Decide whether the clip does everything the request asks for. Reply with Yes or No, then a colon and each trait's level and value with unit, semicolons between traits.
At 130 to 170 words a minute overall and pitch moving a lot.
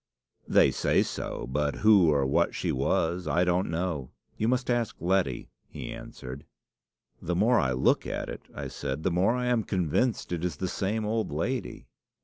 No: average, 180 wpm; wide, 6.0 semitones